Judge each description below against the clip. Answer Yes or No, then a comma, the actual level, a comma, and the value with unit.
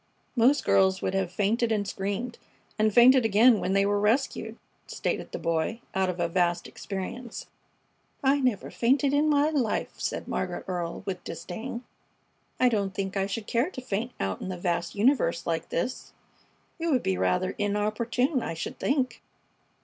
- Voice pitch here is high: Yes, high, 210 Hz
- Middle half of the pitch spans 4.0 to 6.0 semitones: Yes, average, 4.9 semitones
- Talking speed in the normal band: Yes, average, 170 wpm